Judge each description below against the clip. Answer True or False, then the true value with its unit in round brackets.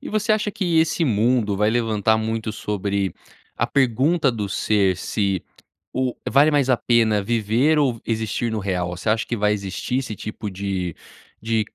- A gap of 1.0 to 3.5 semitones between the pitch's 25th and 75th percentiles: False (4.0 semitones)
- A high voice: False (110 Hz)